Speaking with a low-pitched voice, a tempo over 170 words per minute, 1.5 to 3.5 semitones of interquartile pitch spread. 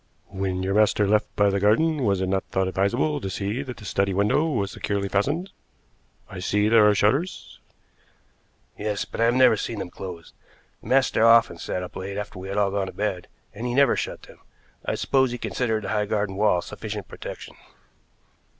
Yes: low, 105 Hz; average, 200 wpm; average, 3.1 semitones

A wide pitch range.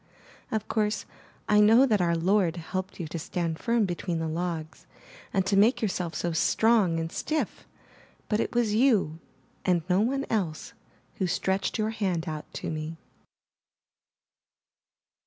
No: average, 4.5 semitones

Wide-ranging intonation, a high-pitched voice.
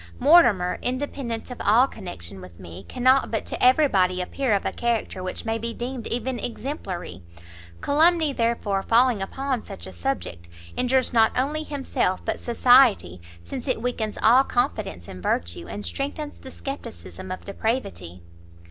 Yes: wide, 6.3 semitones; high, 230 Hz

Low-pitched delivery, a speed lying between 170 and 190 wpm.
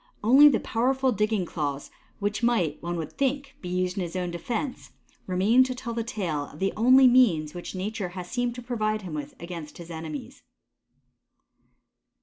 No: high, 205 Hz; average, 175 wpm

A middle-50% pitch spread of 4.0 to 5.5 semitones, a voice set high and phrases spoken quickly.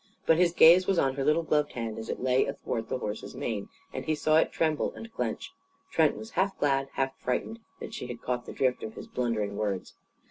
No: average, 5.2 semitones; low, 135 Hz; fast, 225 wpm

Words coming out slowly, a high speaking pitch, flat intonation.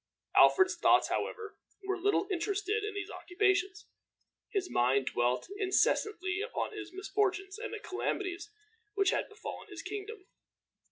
Yes: slow, 130 wpm; very high, 390 Hz; narrow, 2.2 semitones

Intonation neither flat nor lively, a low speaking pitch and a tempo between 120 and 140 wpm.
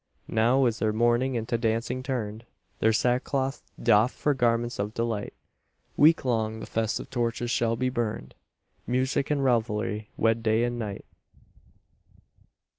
No: narrow, 2.3 semitones; low, 115 Hz; slow, 135 wpm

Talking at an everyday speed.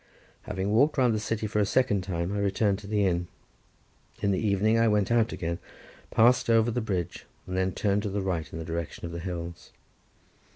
No: fast, 210 wpm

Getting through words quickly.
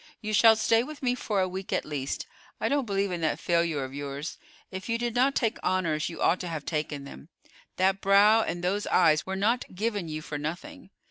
Yes: fast, 220 wpm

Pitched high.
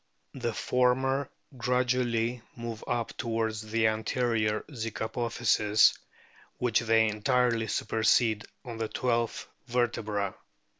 No: low, 115 Hz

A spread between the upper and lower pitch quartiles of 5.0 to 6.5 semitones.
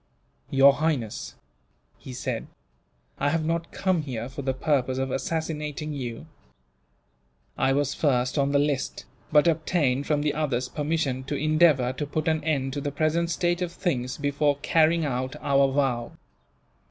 No: average, 3.0 semitones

